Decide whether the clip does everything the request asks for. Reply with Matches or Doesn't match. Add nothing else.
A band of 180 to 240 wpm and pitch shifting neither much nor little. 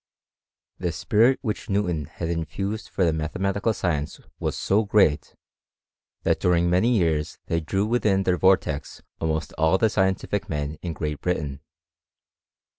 Doesn't match